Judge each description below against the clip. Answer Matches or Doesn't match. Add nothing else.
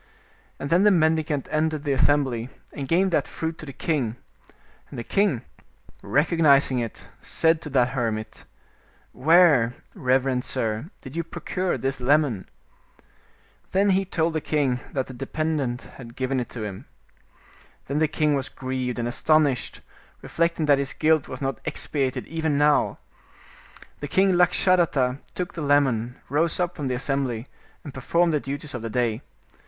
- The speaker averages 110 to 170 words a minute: Matches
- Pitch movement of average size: Matches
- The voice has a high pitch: Doesn't match